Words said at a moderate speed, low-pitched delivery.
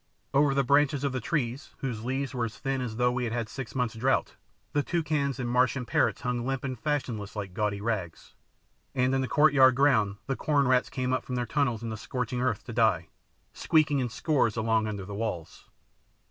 No: fast, 215 wpm; low, 125 Hz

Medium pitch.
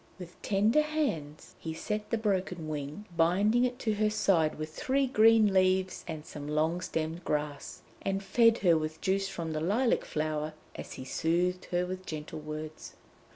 Yes: medium, 180 Hz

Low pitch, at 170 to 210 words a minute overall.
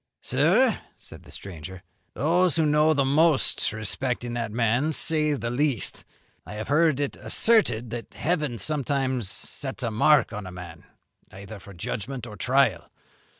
No: low, 130 Hz; average, 150 wpm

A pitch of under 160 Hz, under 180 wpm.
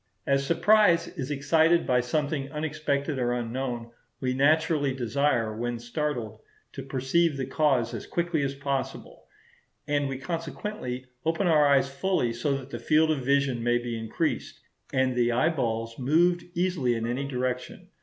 Yes: low, 135 Hz; average, 155 wpm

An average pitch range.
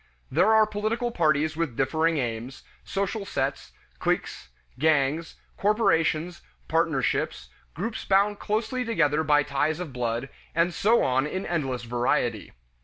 No: wide, 6.7 semitones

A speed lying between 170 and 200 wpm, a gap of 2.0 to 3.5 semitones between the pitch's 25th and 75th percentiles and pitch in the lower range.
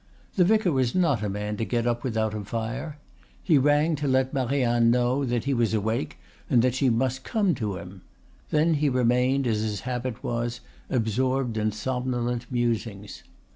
Yes: average, 175 wpm; average, 3.0 semitones; low, 120 Hz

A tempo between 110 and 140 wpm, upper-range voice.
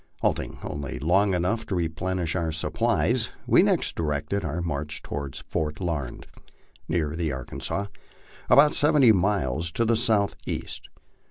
No: slow, 135 wpm; very low, 85 Hz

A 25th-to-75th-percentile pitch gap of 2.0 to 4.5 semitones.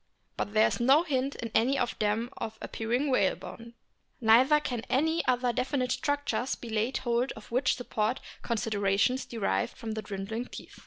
Yes: average, 2.9 semitones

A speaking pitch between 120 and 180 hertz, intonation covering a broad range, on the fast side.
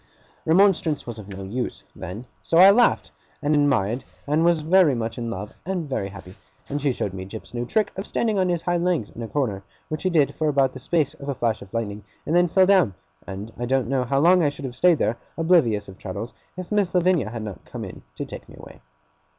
Yes: medium, 140 Hz; wide, 7.5 semitones; fast, 240 wpm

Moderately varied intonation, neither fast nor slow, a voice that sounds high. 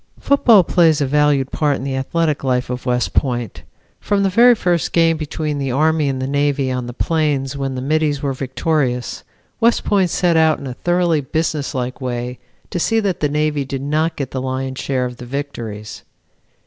No: average, 3.6 semitones; average, 190 wpm; medium, 145 Hz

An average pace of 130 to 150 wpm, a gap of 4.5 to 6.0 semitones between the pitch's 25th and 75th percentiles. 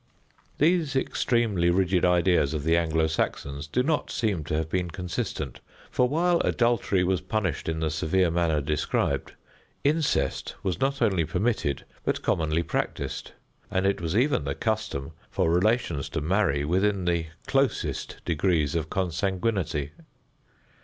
Yes: average, 140 wpm; wide, 5.4 semitones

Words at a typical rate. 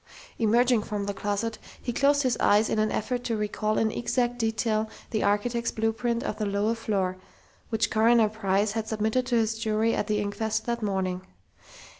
Yes: average, 180 wpm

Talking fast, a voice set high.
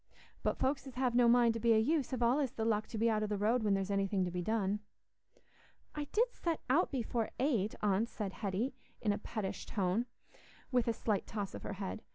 Yes: fast, 225 wpm; high, 225 Hz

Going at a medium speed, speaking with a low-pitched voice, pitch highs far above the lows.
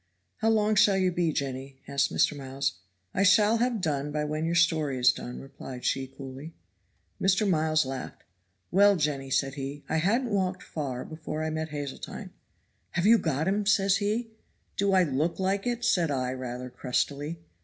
No: average, 175 wpm; medium, 155 Hz; wide, 6.0 semitones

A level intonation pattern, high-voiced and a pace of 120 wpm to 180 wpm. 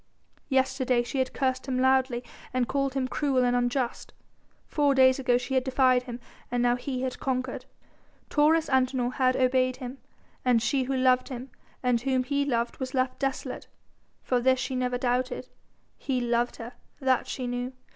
Yes: narrow, 1.2 semitones; very high, 255 Hz; average, 175 wpm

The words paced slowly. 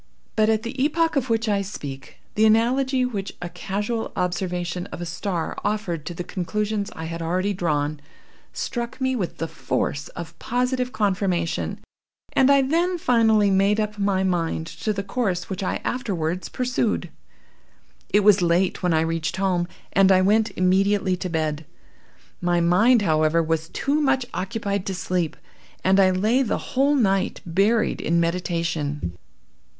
No: average, 160 wpm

